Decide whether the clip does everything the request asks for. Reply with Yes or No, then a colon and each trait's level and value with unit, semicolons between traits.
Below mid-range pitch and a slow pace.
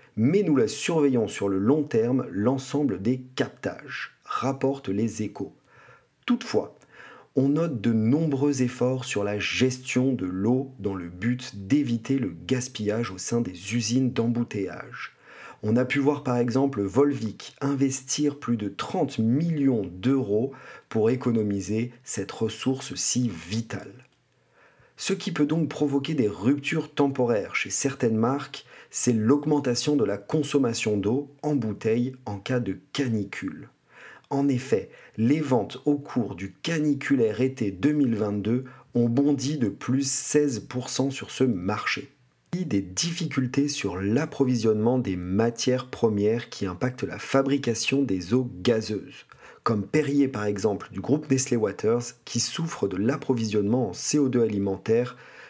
Yes: low, 125 Hz; slow, 135 wpm